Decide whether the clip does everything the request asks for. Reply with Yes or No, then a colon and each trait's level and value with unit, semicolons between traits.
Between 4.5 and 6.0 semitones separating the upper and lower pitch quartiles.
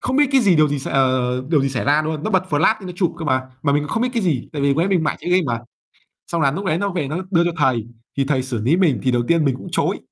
Yes: average, 4.9 semitones